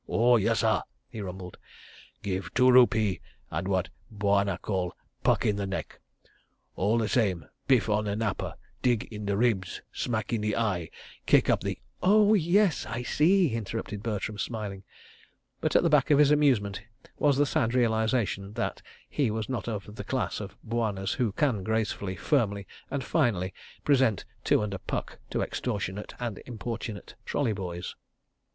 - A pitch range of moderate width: Yes, average, 3.7 semitones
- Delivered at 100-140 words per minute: No, average, 160 wpm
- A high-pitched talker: No, low, 110 Hz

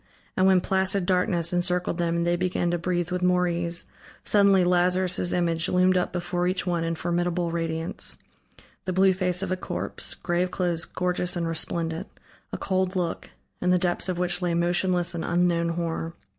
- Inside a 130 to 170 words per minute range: No, average, 180 wpm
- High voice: No, medium, 175 Hz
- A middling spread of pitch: No, narrow, 1.1 semitones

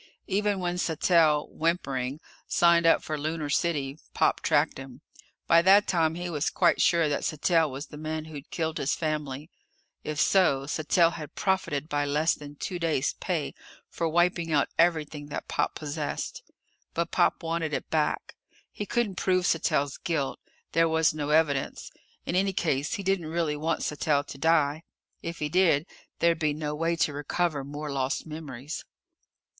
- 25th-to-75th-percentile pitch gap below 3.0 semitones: Yes, narrow, 2.6 semitones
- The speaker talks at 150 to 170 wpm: Yes, average, 165 wpm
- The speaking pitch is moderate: Yes, medium, 155 Hz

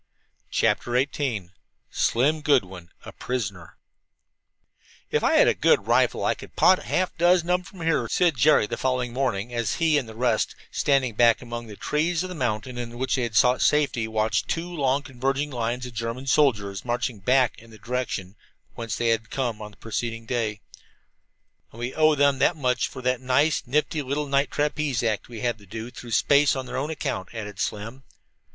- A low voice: Yes, low, 125 Hz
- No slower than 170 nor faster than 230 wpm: Yes, average, 195 wpm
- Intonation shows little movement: No, average, 3.8 semitones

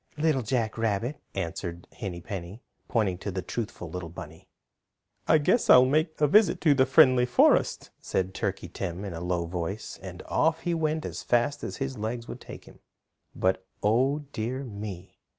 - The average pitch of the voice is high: No, low, 110 Hz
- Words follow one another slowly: No, average, 175 wpm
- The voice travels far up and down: Yes, wide, 6.7 semitones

